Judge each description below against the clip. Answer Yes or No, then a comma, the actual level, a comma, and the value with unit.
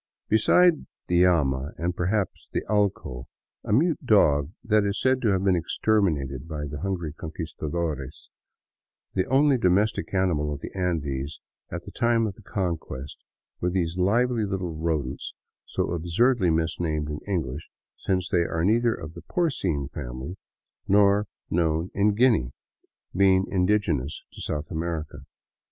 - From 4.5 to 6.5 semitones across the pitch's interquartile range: Yes, average, 5.1 semitones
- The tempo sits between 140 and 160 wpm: Yes, average, 145 wpm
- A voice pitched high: No, very low, 90 Hz